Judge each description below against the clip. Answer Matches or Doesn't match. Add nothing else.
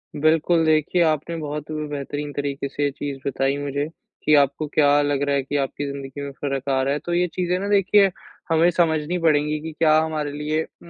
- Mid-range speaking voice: Matches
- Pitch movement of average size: Doesn't match